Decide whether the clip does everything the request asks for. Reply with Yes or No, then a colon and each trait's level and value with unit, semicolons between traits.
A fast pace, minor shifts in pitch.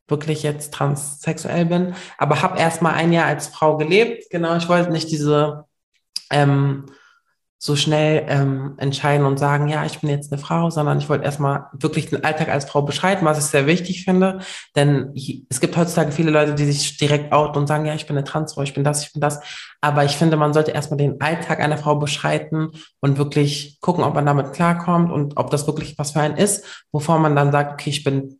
Yes: fast, 215 wpm; narrow, 2.0 semitones